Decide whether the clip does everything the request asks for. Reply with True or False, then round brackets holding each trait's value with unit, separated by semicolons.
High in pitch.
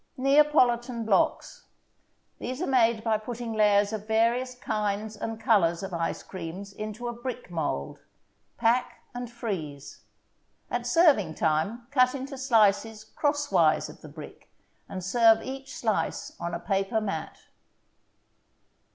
True (220 Hz)